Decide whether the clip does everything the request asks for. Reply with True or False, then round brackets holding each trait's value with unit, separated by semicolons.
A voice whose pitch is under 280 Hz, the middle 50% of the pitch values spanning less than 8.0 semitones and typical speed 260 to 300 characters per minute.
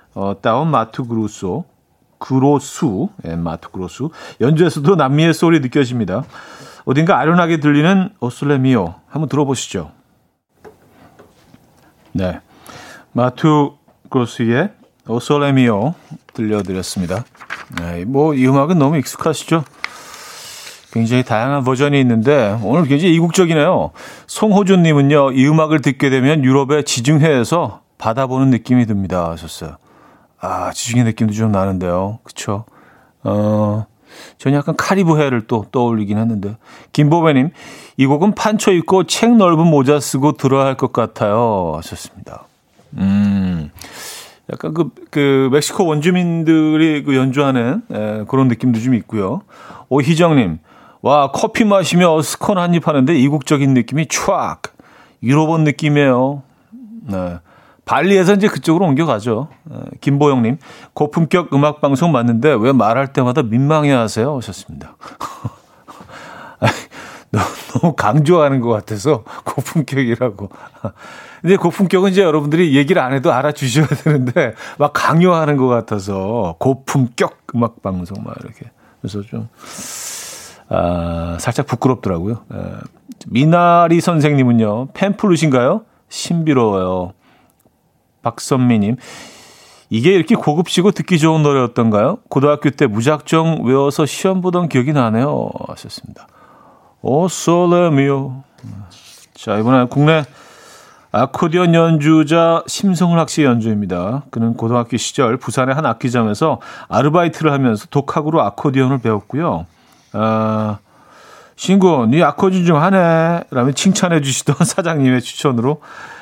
True (140 Hz; 5.6 semitones; 290 characters per minute)